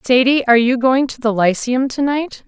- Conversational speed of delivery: Yes, average, 195 wpm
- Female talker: Yes, female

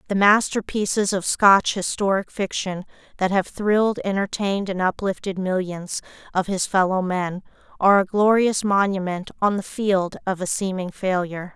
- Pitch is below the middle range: No, high, 195 Hz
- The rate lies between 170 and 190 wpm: No, average, 145 wpm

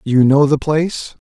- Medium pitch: Yes, medium, 145 Hz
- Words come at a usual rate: Yes, average, 190 wpm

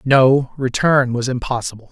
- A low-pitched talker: Yes, low, 130 Hz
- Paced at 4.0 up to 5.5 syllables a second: Yes, 4.5 syllables/s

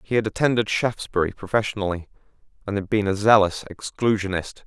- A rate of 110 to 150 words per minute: Yes, average, 140 wpm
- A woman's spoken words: No, male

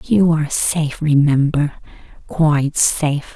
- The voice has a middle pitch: Yes, medium, 150 Hz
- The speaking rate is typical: No, slow, 90 wpm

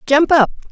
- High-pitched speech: Yes, very high, 295 Hz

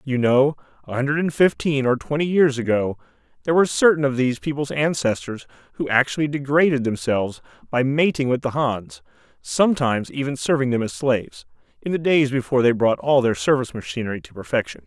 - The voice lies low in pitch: Yes, low, 130 Hz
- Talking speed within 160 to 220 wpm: Yes, average, 180 wpm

